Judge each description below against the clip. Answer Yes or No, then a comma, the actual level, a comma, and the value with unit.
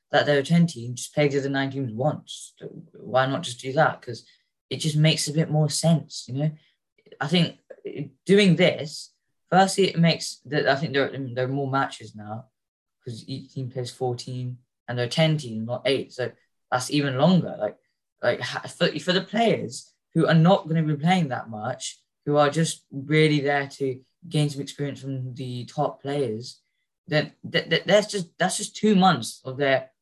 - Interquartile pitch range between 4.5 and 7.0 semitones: No, average, 4.0 semitones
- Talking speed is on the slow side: No, average, 185 wpm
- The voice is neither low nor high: Yes, medium, 145 Hz